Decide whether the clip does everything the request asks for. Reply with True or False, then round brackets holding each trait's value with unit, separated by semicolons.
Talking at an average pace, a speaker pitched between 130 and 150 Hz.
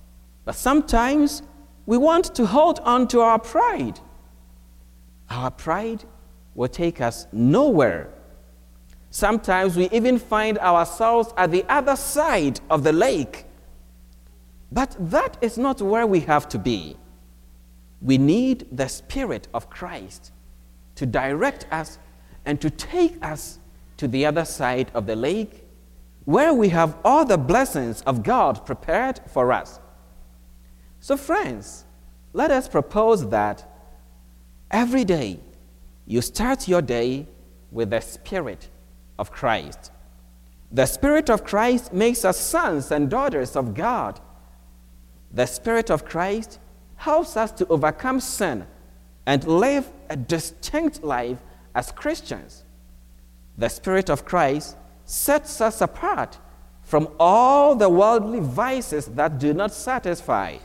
False (125 wpm; 140 Hz)